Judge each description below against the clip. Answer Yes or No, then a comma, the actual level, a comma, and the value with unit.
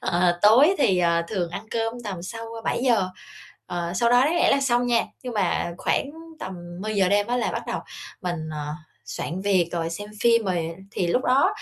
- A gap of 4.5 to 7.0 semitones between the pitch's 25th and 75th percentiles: Yes, wide, 5.5 semitones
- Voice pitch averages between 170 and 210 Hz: Yes, high, 205 Hz